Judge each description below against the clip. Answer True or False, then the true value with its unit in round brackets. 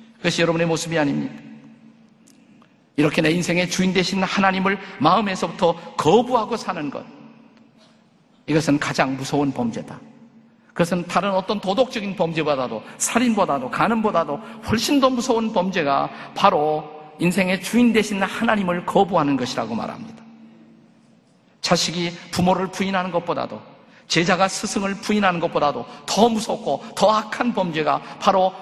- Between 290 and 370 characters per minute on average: True (320 characters per minute)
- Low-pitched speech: False (190 Hz)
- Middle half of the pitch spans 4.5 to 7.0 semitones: True (5.1 semitones)